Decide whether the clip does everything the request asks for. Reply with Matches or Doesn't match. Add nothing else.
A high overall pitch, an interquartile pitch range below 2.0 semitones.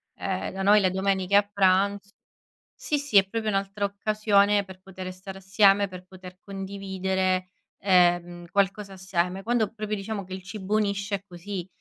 Matches